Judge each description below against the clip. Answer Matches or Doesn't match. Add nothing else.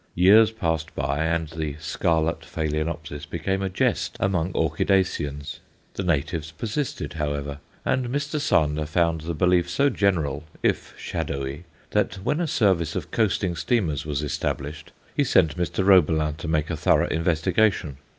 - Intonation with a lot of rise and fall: Doesn't match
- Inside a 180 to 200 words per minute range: Doesn't match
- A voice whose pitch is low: Matches